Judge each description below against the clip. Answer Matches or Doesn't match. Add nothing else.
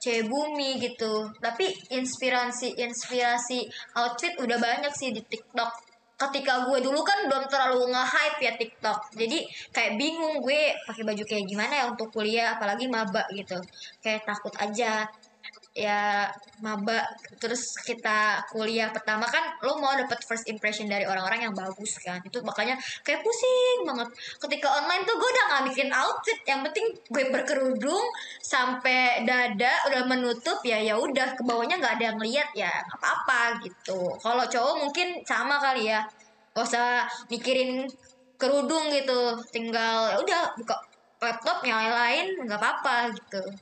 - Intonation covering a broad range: Doesn't match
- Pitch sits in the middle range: Doesn't match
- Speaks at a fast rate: Matches